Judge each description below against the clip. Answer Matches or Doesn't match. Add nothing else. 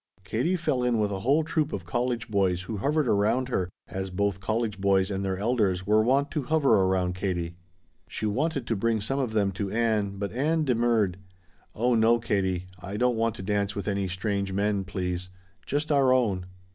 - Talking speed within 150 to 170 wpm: Doesn't match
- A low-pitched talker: Matches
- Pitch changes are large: Doesn't match